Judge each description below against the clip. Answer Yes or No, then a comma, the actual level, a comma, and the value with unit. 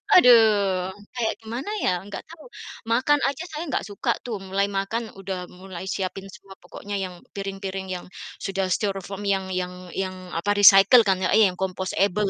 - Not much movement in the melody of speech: Yes, narrow, 2.3 semitones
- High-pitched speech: Yes, high, 195 Hz